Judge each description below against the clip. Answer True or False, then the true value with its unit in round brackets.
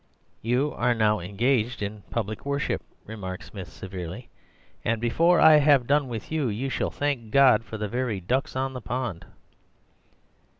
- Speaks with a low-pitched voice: True (120 Hz)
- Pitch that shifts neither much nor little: True (4.2 semitones)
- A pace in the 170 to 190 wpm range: False (160 wpm)